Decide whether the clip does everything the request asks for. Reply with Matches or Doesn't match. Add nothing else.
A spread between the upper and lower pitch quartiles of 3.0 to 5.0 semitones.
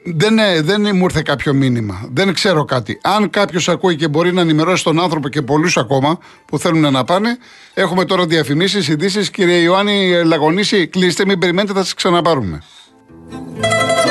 Matches